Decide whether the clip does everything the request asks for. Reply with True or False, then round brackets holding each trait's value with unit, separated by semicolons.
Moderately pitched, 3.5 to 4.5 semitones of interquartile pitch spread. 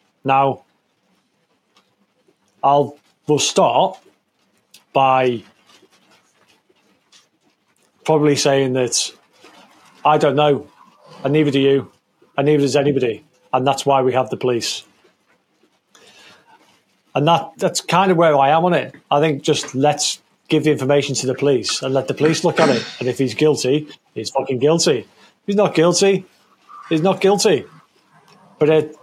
False (145 Hz; 2.9 semitones)